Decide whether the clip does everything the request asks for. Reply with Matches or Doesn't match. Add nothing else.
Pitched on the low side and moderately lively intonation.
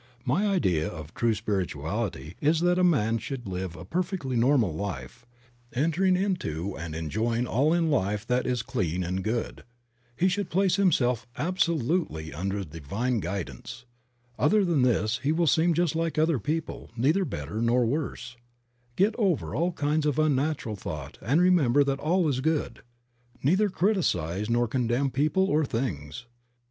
Doesn't match